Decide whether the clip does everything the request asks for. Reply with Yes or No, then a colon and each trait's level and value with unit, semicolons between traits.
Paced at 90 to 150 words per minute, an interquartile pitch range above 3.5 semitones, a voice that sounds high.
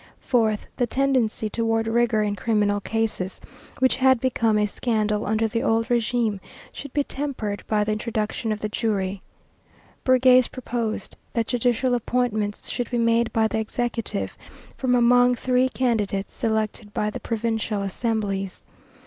No: average, 145 wpm; narrow, 2.5 semitones; high, 225 Hz